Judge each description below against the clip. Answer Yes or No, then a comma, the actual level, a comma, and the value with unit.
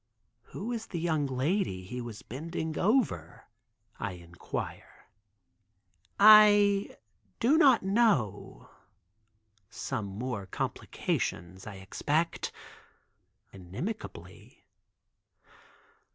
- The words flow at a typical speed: No, slow, 80 wpm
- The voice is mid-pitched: Yes, medium, 145 Hz